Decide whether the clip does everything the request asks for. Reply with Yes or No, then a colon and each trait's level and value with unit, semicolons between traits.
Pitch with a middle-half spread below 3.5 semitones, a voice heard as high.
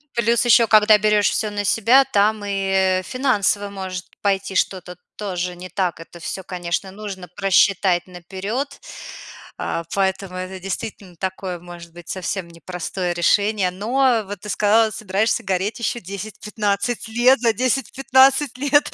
Yes: average, 3.0 semitones; high, 200 Hz